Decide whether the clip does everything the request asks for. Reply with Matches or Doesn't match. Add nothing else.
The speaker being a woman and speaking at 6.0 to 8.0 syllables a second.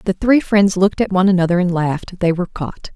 Matches